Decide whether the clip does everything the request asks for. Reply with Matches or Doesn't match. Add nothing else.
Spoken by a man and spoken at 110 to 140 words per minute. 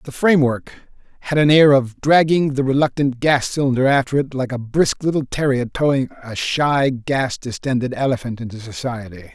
Doesn't match